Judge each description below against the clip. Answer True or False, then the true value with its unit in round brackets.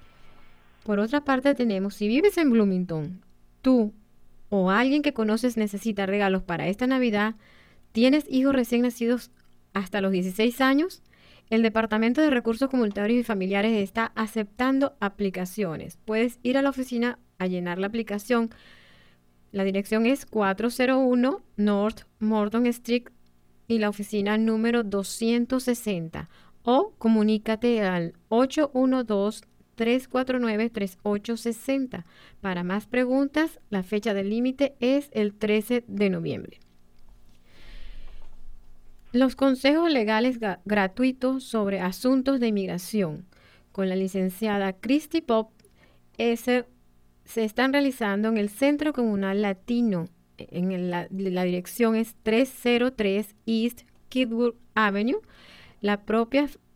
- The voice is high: True (220 Hz)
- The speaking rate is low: True (115 wpm)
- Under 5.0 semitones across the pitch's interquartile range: True (4.2 semitones)